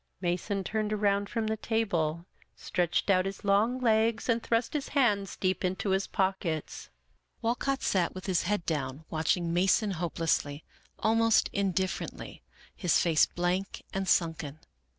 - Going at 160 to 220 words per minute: No, average, 145 wpm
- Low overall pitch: No, high, 195 Hz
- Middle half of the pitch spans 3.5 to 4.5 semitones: Yes, average, 4.0 semitones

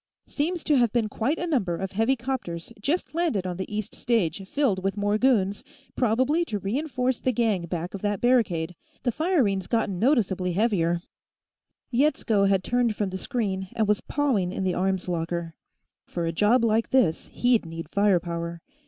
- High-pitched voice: Yes, high, 210 Hz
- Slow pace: No, average, 185 wpm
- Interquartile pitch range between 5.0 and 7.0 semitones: Yes, average, 5.3 semitones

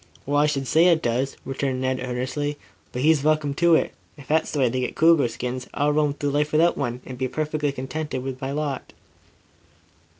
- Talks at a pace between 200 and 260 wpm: Yes, fast, 205 wpm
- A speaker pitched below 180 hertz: Yes, medium, 140 Hz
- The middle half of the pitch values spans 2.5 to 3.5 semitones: Yes, average, 2.8 semitones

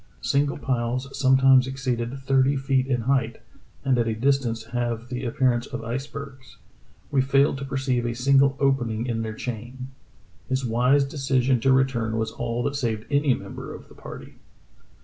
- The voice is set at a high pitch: No, low, 130 Hz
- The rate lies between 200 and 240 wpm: No, average, 170 wpm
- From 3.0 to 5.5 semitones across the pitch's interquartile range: No, narrow, 2.4 semitones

